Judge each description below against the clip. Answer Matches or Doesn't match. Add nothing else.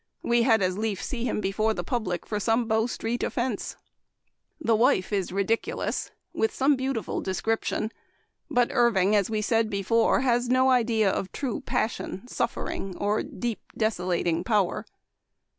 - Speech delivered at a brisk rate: Doesn't match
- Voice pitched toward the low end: Doesn't match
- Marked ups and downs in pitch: Doesn't match